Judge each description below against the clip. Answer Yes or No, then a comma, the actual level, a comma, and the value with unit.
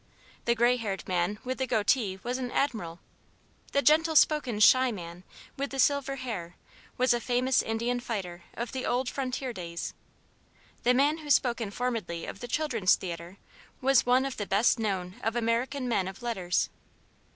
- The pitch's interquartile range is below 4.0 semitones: No, average, 4.8 semitones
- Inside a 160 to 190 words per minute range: Yes, average, 170 wpm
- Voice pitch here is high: Yes, high, 240 Hz